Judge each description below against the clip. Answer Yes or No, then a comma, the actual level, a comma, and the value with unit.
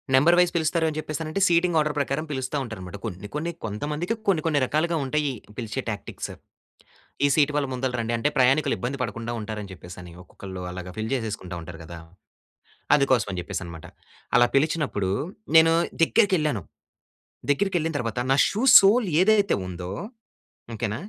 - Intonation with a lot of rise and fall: Yes, wide, 7.1 semitones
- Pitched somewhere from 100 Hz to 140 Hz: Yes, low, 135 Hz